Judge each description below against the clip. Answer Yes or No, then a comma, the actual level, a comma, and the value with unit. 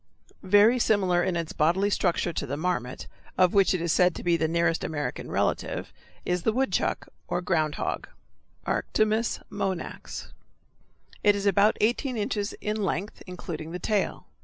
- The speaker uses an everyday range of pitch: Yes, average, 3.5 semitones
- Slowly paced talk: No, average, 160 wpm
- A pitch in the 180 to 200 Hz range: Yes, medium, 185 Hz